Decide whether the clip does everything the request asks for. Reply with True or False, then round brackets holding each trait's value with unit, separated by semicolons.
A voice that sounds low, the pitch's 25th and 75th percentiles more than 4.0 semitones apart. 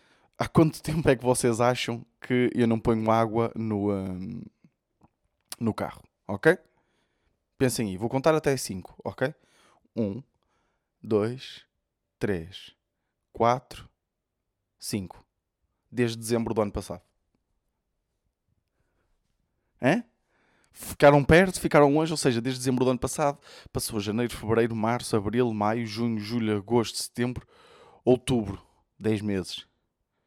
False (115 Hz; 3.7 semitones)